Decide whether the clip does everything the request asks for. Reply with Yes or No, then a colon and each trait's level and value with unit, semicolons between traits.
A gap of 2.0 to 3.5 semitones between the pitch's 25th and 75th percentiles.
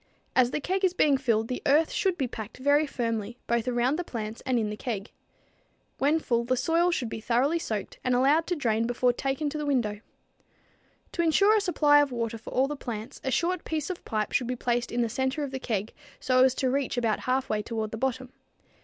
No: average, 4.0 semitones